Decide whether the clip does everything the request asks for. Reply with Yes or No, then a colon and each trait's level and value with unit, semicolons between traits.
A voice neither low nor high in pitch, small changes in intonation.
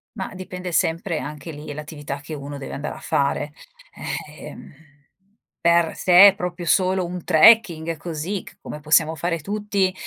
No: medium, 165 Hz; average, 3.4 semitones